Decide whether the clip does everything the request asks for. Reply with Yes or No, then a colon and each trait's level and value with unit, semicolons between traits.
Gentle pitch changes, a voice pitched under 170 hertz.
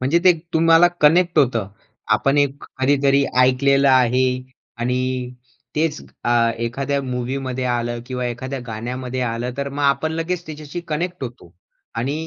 No: average, 3.2 semitones; low, 135 Hz